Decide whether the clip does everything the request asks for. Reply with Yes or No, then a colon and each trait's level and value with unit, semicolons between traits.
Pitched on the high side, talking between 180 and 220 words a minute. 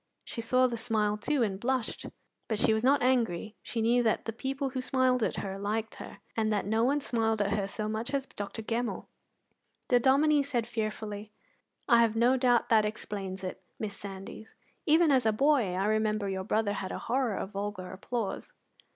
Yes: high, 225 Hz; average, 195 wpm